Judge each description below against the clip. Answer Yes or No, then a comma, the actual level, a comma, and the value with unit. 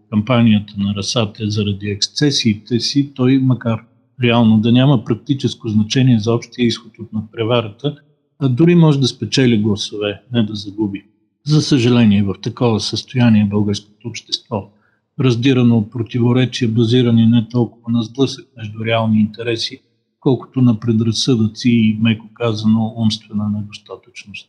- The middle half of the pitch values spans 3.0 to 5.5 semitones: No, narrow, 2.4 semitones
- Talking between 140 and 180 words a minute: No, average, 130 wpm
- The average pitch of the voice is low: Yes, low, 115 Hz